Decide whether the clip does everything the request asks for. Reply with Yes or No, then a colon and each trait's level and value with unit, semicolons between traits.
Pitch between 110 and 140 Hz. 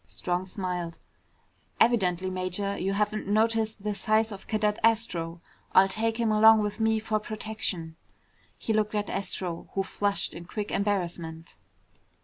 No: high, 205 Hz